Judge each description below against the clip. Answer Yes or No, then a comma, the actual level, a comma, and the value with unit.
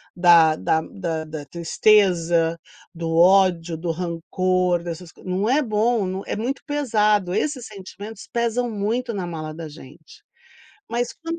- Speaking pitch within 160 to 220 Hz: Yes, medium, 185 Hz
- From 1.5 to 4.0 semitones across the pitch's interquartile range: No, average, 5.0 semitones